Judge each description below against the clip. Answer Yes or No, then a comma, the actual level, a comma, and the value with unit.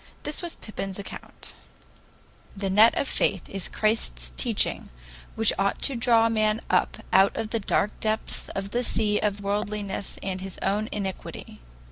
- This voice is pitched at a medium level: No, high, 210 Hz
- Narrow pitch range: Yes, narrow, 2.2 semitones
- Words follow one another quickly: No, average, 155 wpm